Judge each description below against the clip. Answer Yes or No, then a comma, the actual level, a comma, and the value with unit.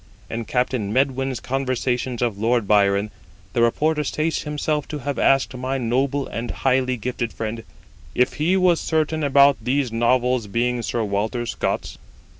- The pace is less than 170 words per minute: Yes, average, 150 wpm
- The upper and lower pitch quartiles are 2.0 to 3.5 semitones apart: Yes, average, 3.1 semitones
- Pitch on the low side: Yes, low, 125 Hz